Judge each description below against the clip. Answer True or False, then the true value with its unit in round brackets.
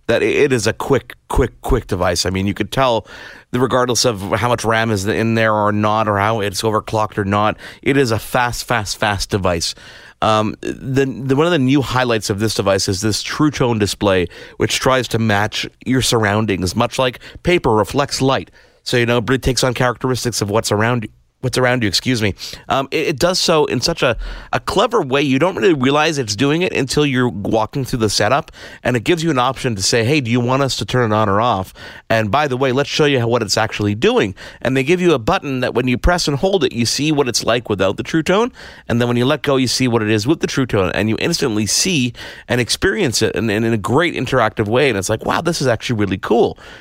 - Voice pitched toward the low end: True (120 Hz)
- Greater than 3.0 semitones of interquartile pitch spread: True (3.8 semitones)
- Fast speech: True (250 wpm)